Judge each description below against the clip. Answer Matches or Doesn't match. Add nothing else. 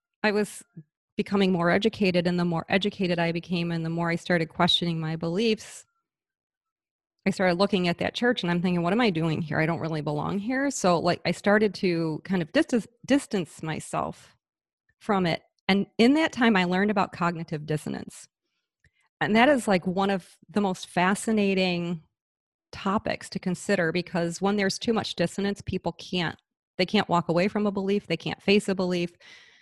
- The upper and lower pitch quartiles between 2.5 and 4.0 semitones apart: Matches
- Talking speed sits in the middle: Matches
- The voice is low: Doesn't match